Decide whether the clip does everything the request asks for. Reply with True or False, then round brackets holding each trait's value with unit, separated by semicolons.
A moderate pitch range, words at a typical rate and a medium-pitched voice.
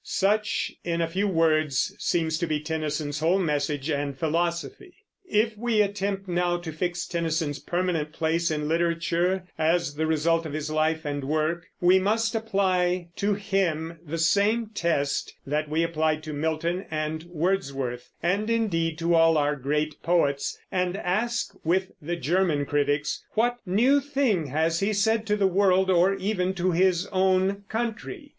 True (3.9 semitones; 160 wpm; 170 Hz)